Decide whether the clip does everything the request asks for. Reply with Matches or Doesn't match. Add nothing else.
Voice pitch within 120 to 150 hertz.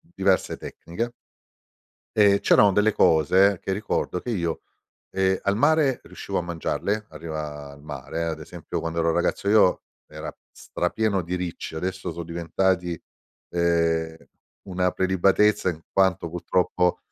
Doesn't match